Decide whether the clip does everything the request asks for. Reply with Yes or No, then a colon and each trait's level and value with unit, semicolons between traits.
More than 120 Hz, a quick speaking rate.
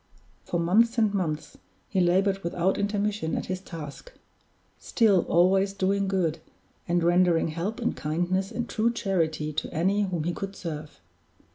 No: medium, 185 Hz; average, 150 wpm